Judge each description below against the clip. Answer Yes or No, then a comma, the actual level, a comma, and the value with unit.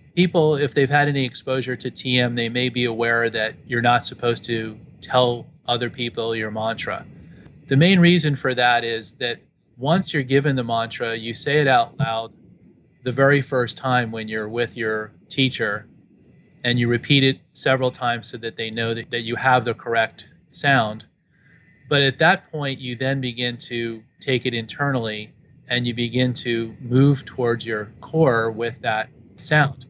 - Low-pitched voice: Yes, low, 125 Hz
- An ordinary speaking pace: Yes, average, 175 wpm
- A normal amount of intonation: Yes, average, 3.2 semitones